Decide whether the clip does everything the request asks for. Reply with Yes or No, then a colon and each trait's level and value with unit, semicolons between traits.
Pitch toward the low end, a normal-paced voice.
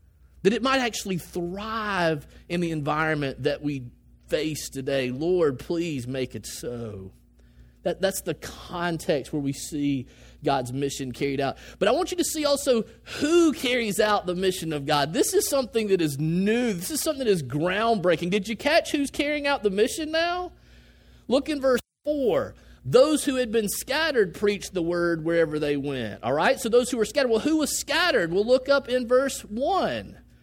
No: medium, 185 Hz; average, 185 wpm